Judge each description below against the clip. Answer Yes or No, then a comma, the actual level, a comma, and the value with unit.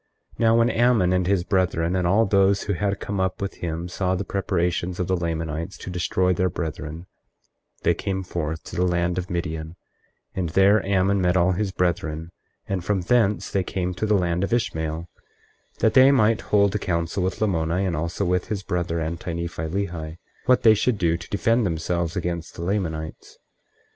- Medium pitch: No, very low, 90 Hz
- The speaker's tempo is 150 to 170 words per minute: No, average, 195 wpm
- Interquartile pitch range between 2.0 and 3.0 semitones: Yes, average, 2.7 semitones